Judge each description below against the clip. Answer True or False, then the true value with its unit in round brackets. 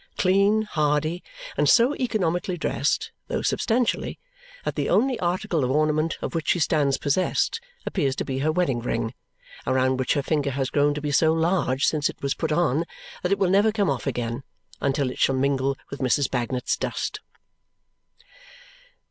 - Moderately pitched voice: True (150 Hz)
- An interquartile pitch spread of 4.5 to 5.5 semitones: True (4.9 semitones)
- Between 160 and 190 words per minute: True (175 wpm)